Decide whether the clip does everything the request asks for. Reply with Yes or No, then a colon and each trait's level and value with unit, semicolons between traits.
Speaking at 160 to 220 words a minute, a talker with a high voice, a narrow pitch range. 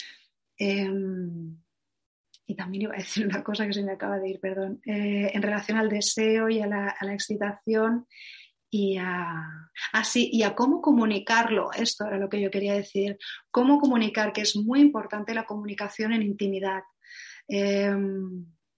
Yes: average, 165 wpm; high, 205 Hz; narrow, 2.0 semitones